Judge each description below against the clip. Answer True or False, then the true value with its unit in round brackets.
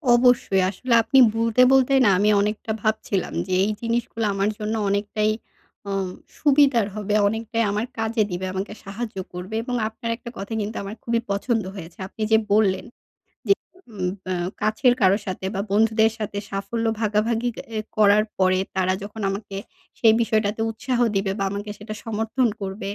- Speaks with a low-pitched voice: False (215 Hz)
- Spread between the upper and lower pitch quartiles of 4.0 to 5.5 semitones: False (2.5 semitones)